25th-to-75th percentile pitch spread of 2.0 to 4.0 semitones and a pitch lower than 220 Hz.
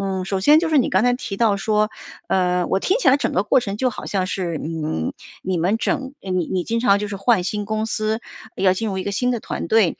Yes: average, 3.5 semitones; high, 200 Hz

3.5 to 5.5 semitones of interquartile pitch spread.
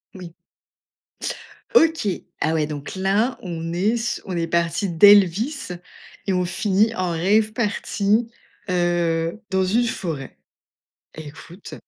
Yes: average, 4.2 semitones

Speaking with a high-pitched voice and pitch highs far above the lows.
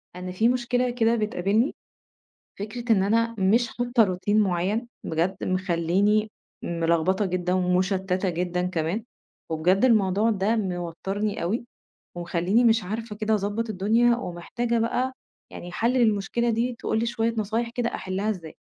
No: high, 205 Hz; average, 4.1 semitones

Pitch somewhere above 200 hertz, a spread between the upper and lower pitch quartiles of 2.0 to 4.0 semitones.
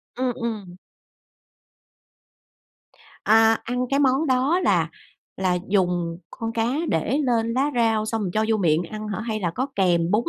No: high, 220 Hz; average, 4.7 semitones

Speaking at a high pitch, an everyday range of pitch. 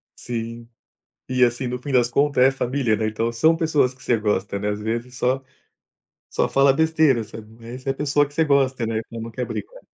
No: low, 125 Hz; average, 3.4 semitones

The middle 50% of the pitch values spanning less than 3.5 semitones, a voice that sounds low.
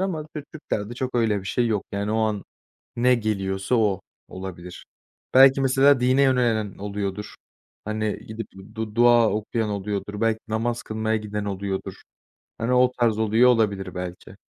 Yes: average, 3.0 semitones; low, 110 Hz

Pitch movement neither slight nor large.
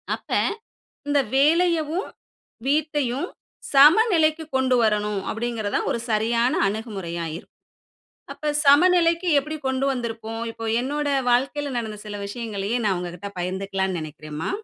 No: wide, 6.3 semitones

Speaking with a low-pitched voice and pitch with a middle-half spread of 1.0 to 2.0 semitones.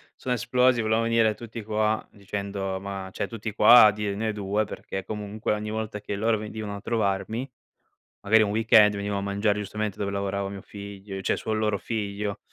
Yes: low, 105 Hz; narrow, 1.7 semitones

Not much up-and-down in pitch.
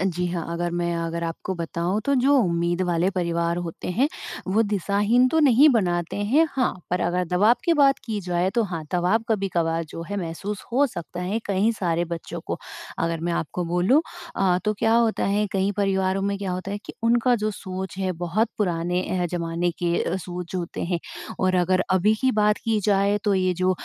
No: average, 3.3 semitones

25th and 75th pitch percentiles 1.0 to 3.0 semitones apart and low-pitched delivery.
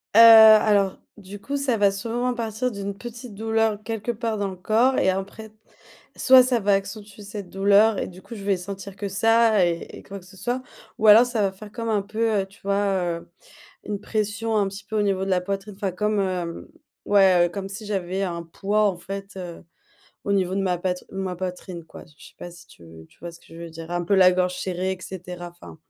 No: average, 2.7 semitones; high, 200 Hz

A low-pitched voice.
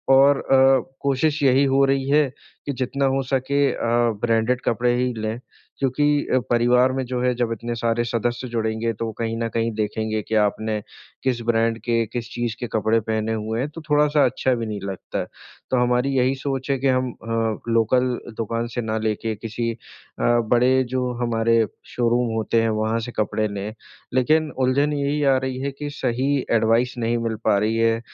Yes: low, 120 Hz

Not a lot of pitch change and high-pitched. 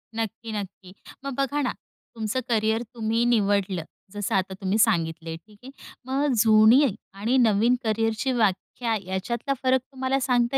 No: average, 3.8 semitones; high, 220 Hz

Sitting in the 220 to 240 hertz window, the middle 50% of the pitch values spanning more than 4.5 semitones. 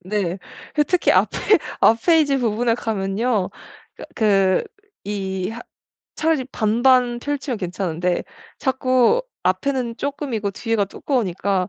Yes: high, 225 Hz; average, 5.1 semitones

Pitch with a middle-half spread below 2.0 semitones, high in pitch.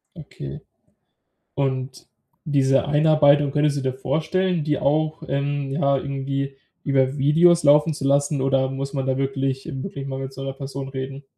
No: narrow, 1.5 semitones; medium, 140 Hz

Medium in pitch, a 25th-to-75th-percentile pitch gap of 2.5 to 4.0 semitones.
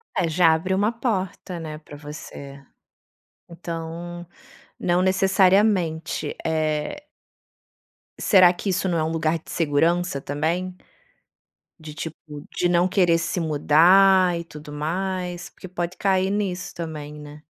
Yes: medium, 170 Hz; average, 2.8 semitones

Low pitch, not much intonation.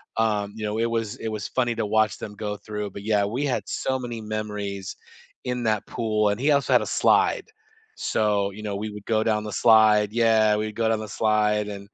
Yes: low, 110 Hz; narrow, 1.4 semitones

